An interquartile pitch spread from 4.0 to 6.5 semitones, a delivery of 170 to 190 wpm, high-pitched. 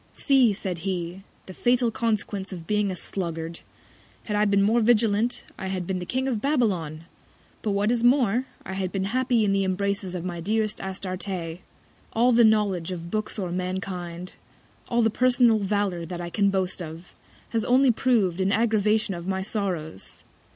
No: average, 3.5 semitones; average, 175 wpm; high, 200 Hz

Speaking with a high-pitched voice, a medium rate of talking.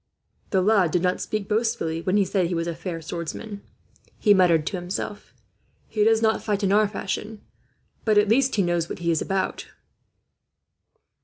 Yes: high, 195 Hz; average, 180 wpm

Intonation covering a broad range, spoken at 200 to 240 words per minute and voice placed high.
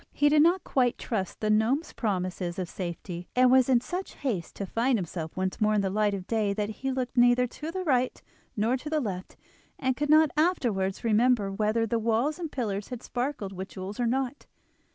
No: average, 4.9 semitones; fast, 205 wpm; high, 230 Hz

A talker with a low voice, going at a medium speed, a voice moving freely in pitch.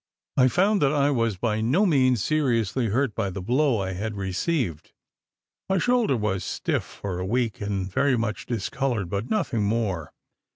Yes: low, 115 Hz; average, 170 wpm; wide, 5.7 semitones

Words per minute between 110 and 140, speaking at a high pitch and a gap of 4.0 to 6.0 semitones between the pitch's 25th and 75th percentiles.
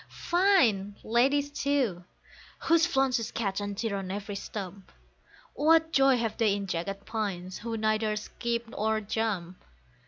Yes: slow, 135 wpm; high, 220 Hz; average, 4.9 semitones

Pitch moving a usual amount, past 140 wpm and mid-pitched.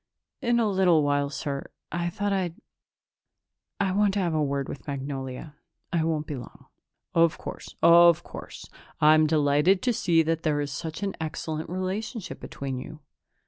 Yes: average, 4.3 semitones; average, 165 wpm; medium, 160 Hz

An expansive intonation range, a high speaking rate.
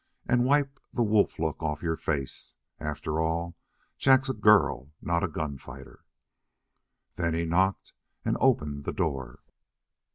No: wide, 6.1 semitones; slow, 135 wpm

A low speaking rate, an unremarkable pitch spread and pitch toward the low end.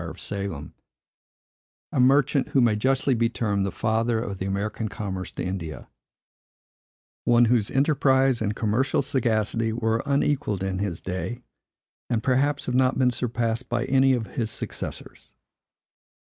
No: average, 145 wpm; average, 4.1 semitones; low, 115 Hz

